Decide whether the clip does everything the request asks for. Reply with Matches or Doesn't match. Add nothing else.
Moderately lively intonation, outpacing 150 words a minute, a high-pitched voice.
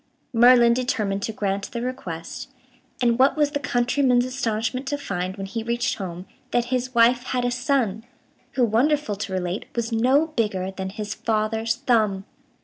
Matches